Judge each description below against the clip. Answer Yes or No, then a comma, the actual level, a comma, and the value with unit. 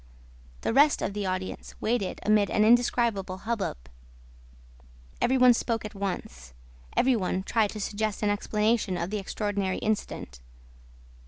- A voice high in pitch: Yes, high, 210 Hz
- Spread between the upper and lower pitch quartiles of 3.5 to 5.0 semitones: No, average, 3.1 semitones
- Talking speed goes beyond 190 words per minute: No, average, 140 wpm